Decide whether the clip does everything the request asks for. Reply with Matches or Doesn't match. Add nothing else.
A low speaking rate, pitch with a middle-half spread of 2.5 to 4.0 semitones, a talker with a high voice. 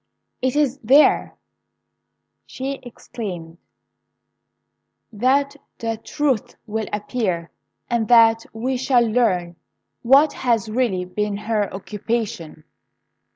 Matches